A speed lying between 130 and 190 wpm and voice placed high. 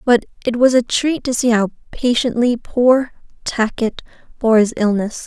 Yes: average, 160 wpm; high, 235 Hz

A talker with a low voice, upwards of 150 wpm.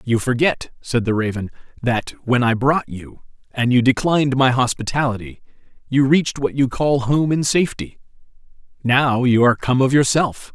Yes: low, 125 Hz; average, 165 wpm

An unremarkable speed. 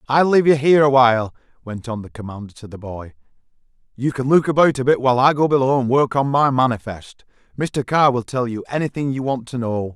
No: fast, 230 wpm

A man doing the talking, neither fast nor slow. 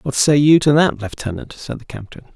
No: male; fast, 230 wpm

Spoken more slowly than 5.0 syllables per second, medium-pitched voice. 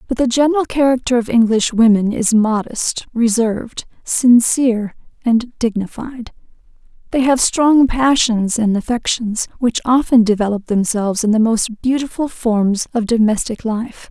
No: 4.6 syllables/s; high, 235 Hz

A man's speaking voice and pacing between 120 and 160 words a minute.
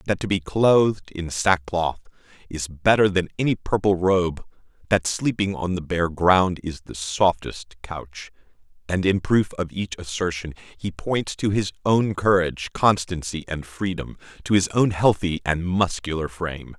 Yes: male; average, 155 wpm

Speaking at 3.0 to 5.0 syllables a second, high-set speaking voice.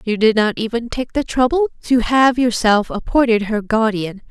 Yes: 4.7 syllables/s; high, 230 Hz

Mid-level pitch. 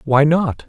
Yes: medium, 150 Hz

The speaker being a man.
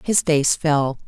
No: female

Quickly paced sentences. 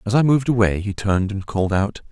Yes: fast, 255 wpm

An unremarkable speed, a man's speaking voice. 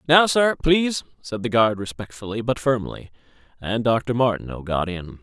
Yes: average, 160 wpm; male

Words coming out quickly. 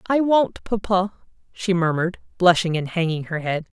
No: average, 160 wpm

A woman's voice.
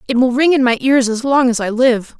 Yes: female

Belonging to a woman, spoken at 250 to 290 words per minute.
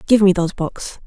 No: female; fast, 225 wpm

